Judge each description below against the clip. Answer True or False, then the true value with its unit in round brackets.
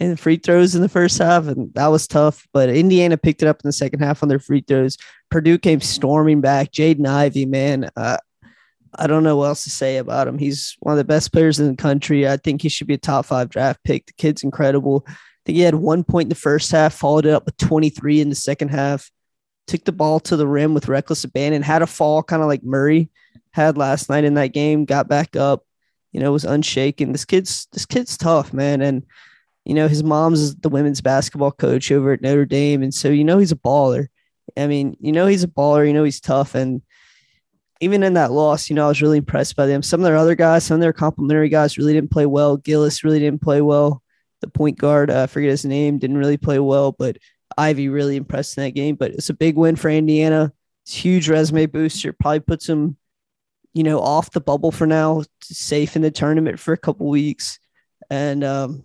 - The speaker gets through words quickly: True (240 wpm)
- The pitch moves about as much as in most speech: False (2.0 semitones)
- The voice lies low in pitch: False (150 Hz)